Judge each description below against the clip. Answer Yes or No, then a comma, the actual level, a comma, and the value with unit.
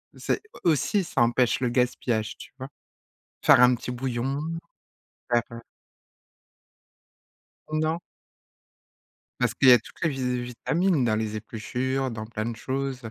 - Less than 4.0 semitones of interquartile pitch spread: Yes, narrow, 2.4 semitones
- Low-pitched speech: Yes, low, 125 Hz